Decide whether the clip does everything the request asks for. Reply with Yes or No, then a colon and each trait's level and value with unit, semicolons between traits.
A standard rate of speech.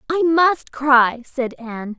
Yes: average, 150 wpm